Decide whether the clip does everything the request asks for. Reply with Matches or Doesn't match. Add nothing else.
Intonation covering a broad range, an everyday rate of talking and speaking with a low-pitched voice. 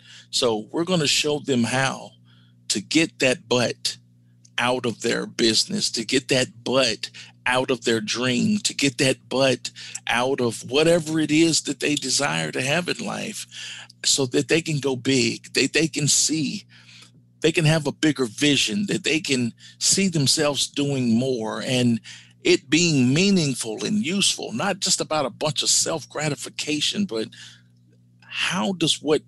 Matches